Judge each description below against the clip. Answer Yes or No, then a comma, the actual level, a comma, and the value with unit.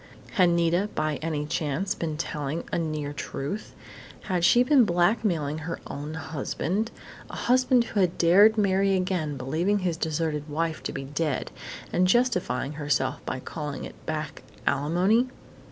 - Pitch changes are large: No, average, 4.4 semitones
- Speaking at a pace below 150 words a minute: No, average, 155 wpm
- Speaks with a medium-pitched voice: Yes, medium, 165 Hz